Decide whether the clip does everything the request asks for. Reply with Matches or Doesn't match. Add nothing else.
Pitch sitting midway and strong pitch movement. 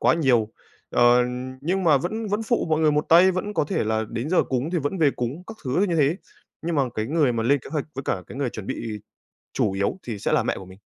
Matches